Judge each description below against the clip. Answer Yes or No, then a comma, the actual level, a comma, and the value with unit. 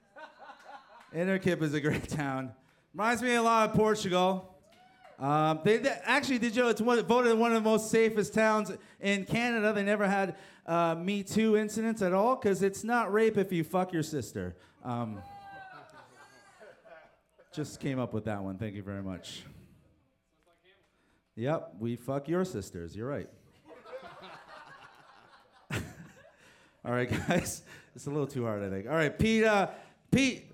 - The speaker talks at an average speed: Yes, average, 155 wpm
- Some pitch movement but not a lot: No, wide, 7.8 semitones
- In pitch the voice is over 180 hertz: Yes, high, 190 Hz